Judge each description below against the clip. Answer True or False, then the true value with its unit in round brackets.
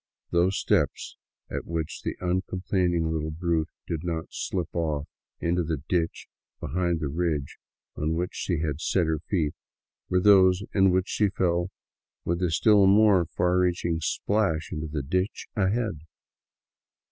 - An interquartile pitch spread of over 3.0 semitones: False (2.6 semitones)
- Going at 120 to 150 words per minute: True (145 wpm)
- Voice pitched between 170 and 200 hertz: False (85 Hz)